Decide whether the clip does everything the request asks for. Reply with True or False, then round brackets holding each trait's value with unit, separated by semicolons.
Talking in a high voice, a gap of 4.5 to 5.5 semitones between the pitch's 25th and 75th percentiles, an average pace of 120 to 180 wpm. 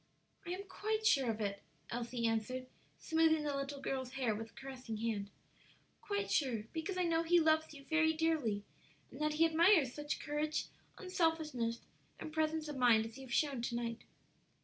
True (290 Hz; 5.2 semitones; 175 wpm)